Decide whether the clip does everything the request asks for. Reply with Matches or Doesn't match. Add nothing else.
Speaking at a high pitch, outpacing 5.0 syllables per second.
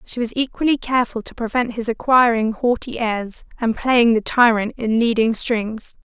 Doesn't match